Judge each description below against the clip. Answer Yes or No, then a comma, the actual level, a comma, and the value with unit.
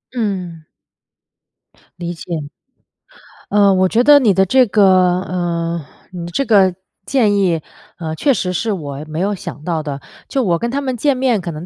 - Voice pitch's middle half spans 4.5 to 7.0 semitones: Yes, average, 5.2 semitones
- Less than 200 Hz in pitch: Yes, medium, 185 Hz